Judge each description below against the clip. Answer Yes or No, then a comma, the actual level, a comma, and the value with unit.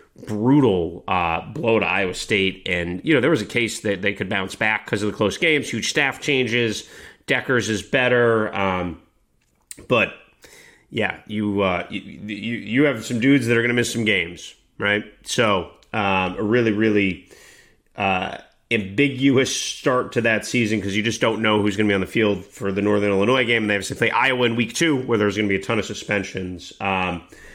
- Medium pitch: No, low, 105 Hz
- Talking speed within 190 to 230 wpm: Yes, fast, 205 wpm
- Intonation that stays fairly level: No, average, 3.4 semitones